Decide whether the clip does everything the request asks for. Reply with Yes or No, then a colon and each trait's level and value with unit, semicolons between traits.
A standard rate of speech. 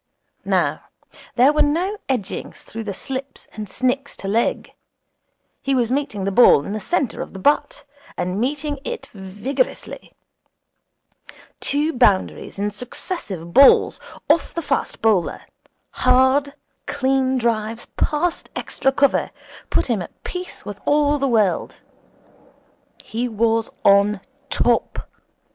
No: slow, 125 wpm